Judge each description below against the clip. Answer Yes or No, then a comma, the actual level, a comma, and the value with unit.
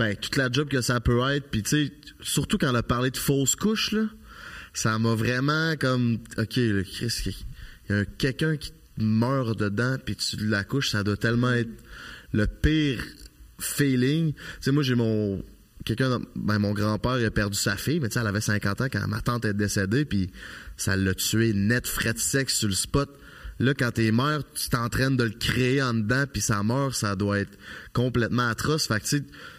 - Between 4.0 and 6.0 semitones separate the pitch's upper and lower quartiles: Yes, average, 4.4 semitones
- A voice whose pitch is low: Yes, low, 120 Hz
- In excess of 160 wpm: Yes, average, 215 wpm